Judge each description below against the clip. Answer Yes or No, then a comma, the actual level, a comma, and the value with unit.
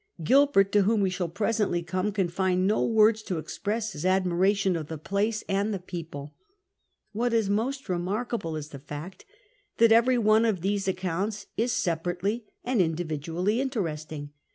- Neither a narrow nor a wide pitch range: Yes, average, 4.0 semitones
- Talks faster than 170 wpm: No, average, 160 wpm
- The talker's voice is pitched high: Yes, high, 195 Hz